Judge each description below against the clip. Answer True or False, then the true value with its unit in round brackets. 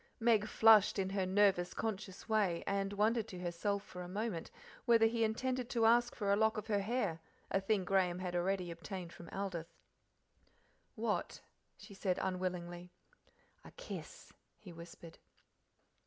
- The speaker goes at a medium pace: True (155 wpm)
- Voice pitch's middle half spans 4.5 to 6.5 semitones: False (3.4 semitones)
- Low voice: False (195 Hz)